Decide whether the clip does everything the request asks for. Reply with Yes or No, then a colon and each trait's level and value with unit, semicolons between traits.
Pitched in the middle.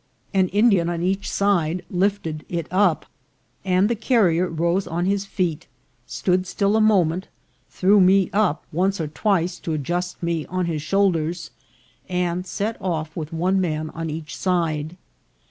Yes: medium, 180 Hz